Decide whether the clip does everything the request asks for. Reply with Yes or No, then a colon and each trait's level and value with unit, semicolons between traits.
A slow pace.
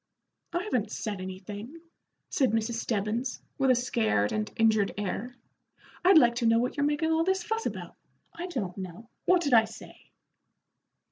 No: average, 165 wpm